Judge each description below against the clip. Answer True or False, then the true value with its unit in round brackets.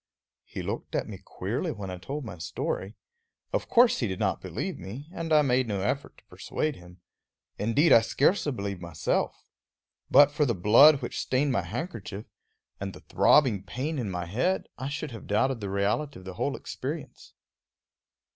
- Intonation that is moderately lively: False (6.8 semitones)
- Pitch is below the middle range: True (115 Hz)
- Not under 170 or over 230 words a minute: True (180 wpm)